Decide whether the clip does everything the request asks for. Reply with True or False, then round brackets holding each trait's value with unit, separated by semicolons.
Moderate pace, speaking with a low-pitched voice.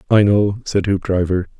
True (150 wpm; 100 Hz)